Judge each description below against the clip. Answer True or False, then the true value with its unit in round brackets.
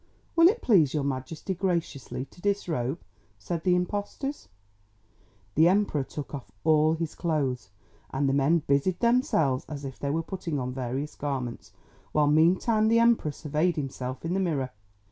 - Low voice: False (155 Hz)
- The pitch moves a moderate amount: True (4.9 semitones)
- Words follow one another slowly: False (160 wpm)